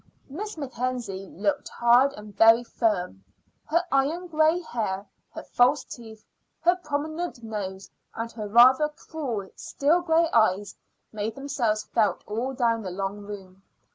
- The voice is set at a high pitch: Yes, high, 235 Hz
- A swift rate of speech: No, average, 140 wpm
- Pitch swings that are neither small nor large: No, wide, 5.9 semitones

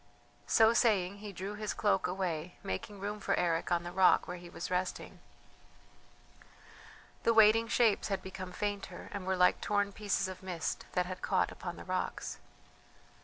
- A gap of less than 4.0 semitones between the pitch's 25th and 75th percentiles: Yes, narrow, 2.5 semitones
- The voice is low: No, high, 190 Hz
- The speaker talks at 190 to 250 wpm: No, average, 170 wpm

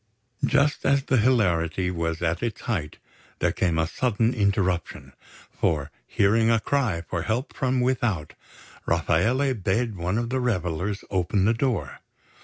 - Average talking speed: Yes, average, 145 wpm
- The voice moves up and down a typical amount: No, wide, 6.1 semitones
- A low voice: Yes, low, 105 Hz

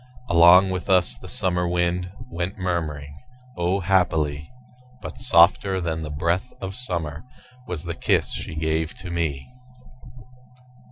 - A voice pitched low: Yes, very low, 85 Hz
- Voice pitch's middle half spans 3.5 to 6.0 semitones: No, narrow, 2.5 semitones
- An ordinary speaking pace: No, slow, 130 wpm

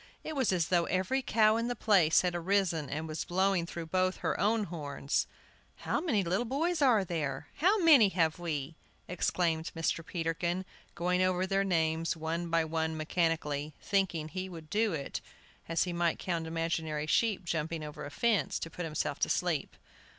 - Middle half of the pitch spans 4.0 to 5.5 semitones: No, average, 3.3 semitones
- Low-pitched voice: No, medium, 170 Hz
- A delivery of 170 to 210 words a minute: Yes, average, 180 wpm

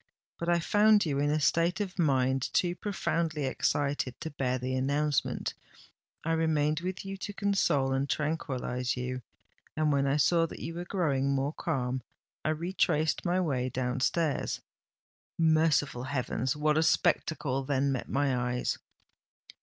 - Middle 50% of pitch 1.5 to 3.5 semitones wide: No, average, 3.9 semitones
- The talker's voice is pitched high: No, medium, 150 Hz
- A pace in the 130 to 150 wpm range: Yes, average, 145 wpm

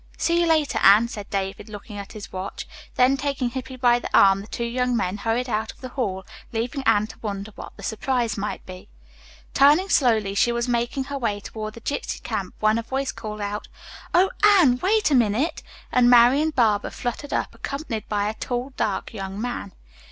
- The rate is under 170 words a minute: No, average, 195 wpm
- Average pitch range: Yes, average, 4.1 semitones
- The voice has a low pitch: No, high, 235 Hz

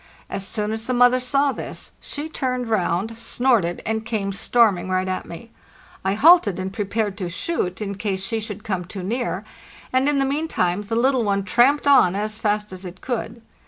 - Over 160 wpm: Yes, average, 195 wpm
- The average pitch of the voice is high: Yes, high, 215 Hz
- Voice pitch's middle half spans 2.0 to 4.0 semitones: No, average, 4.5 semitones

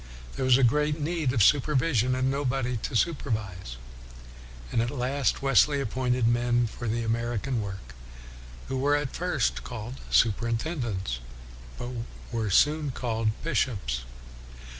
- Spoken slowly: Yes, slow, 125 wpm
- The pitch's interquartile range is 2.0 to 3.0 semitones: No, average, 3.4 semitones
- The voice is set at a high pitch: No, low, 125 Hz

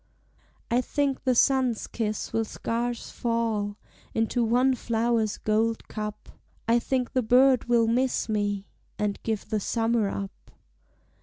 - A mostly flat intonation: Yes, narrow, 2.3 semitones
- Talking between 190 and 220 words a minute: No, slow, 135 wpm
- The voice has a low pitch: No, high, 230 Hz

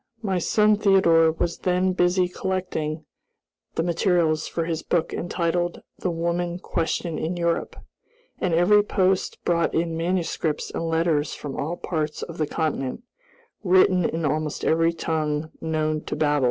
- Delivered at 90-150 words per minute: Yes, average, 145 wpm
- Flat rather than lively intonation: Yes, narrow, 2.2 semitones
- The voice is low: No, medium, 170 Hz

